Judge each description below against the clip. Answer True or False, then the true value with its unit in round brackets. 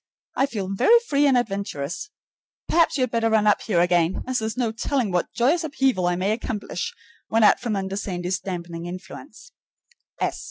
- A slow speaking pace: False (175 wpm)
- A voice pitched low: False (215 Hz)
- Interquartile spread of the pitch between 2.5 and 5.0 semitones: False (5.6 semitones)